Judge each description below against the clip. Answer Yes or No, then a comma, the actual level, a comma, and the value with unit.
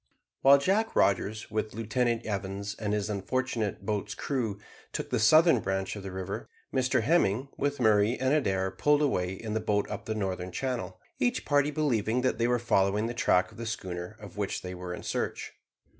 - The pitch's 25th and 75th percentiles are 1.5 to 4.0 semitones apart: No, average, 4.7 semitones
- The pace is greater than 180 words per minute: Yes, average, 190 wpm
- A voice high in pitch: No, low, 110 Hz